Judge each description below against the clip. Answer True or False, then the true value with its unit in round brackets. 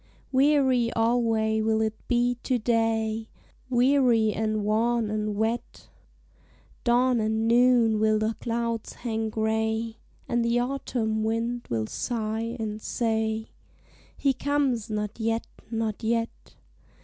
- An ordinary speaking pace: False (120 wpm)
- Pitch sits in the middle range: False (225 Hz)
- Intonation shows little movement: True (1.6 semitones)